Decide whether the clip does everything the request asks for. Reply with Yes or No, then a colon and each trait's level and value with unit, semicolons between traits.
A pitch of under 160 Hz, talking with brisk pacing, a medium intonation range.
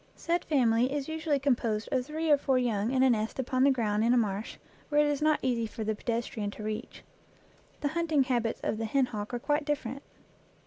No: very high, 255 Hz; fast, 220 wpm; average, 4.5 semitones